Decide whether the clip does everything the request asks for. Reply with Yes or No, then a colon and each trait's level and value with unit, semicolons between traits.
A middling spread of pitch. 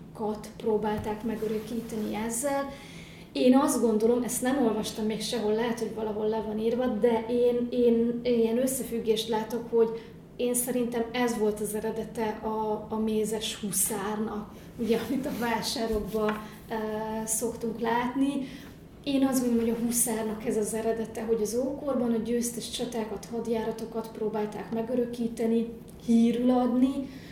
No: narrow, 1.6 semitones